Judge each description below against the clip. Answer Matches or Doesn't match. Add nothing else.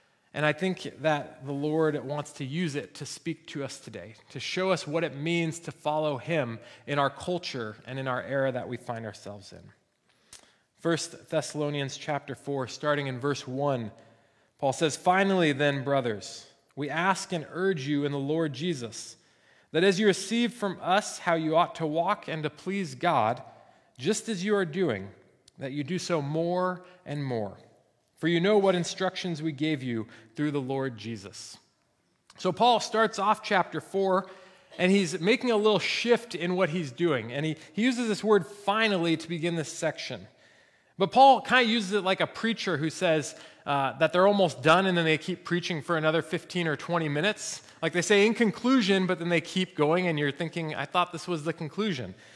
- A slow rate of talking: Doesn't match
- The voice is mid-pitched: Matches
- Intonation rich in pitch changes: Doesn't match